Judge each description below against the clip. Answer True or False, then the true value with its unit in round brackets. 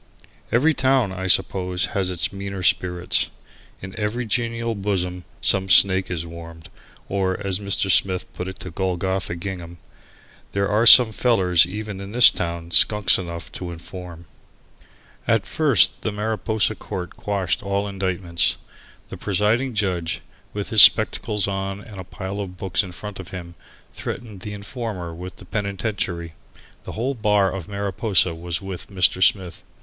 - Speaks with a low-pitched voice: True (95 Hz)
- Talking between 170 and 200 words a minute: False (155 wpm)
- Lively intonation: False (2.6 semitones)